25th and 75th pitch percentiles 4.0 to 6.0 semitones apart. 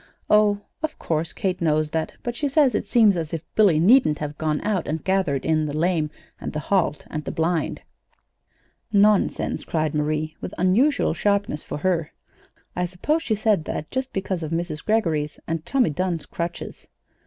Yes: average, 5.0 semitones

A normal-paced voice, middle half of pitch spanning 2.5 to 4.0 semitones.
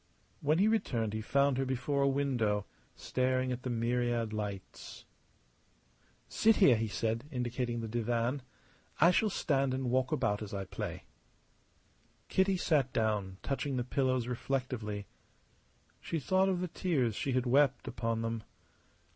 Yes: average, 145 wpm; average, 3.5 semitones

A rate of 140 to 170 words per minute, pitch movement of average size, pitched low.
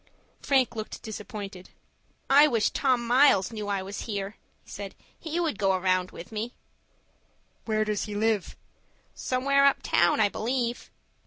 No: average, 150 wpm; average, 4.2 semitones; high, 215 Hz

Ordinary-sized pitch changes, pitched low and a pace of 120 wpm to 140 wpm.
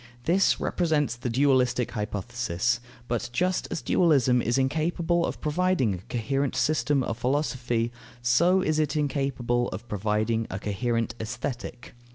Yes: average, 4.3 semitones; low, 125 Hz; slow, 135 wpm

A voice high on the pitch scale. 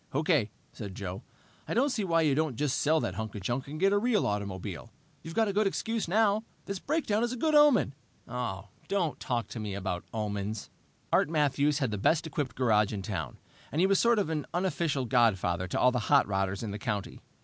No: medium, 140 Hz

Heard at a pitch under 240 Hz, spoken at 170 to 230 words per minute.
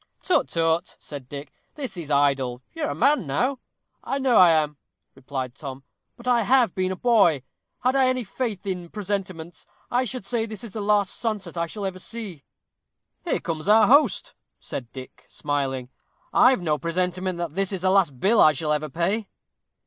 Yes: medium, 185 Hz; average, 185 wpm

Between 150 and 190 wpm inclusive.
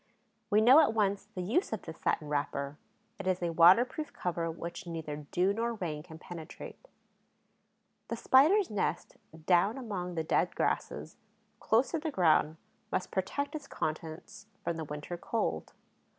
Yes: average, 155 wpm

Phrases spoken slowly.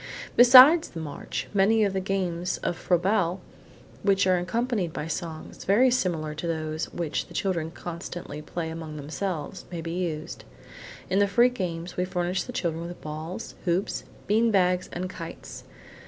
No: average, 160 wpm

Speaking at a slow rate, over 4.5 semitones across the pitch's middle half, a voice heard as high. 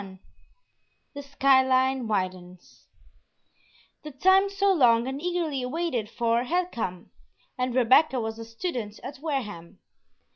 Yes: slow, 130 wpm; average, 5.1 semitones; very high, 255 Hz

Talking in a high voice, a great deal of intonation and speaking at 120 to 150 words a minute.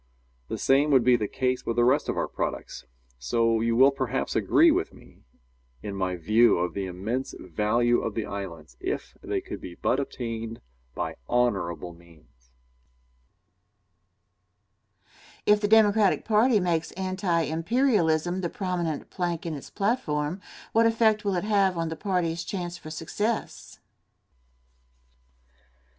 No: medium, 150 Hz; wide, 8.7 semitones; average, 145 wpm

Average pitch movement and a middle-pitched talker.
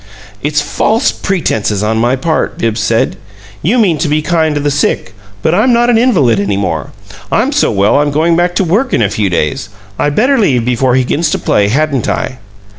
No: wide, 7.8 semitones; medium, 145 Hz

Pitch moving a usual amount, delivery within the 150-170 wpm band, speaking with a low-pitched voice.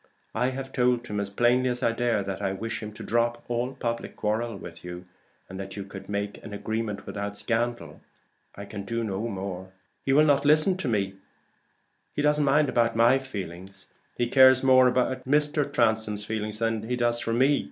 No: average, 4.0 semitones; average, 195 wpm; low, 115 Hz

